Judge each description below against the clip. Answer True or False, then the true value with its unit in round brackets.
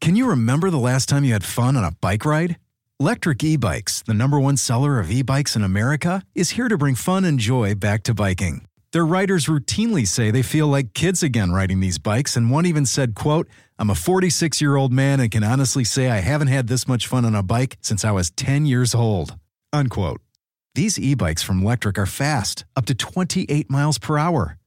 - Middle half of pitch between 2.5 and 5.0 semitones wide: False (5.6 semitones)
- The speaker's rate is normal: False (210 wpm)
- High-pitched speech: False (130 Hz)